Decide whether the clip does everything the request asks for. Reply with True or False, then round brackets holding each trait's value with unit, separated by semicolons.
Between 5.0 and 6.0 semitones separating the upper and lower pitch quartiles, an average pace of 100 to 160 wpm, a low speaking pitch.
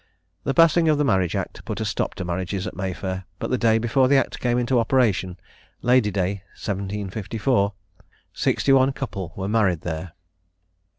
False (5.3 semitones; 180 wpm; 105 Hz)